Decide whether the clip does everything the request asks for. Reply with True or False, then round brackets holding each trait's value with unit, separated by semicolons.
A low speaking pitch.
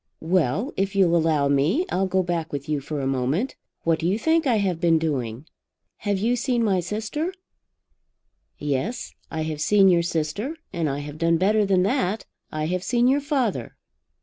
False (180 Hz)